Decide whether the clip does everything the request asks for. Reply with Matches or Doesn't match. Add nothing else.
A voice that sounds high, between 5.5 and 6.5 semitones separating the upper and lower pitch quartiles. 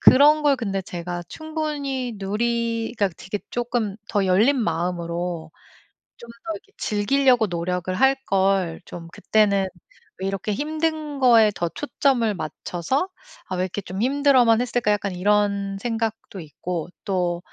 Matches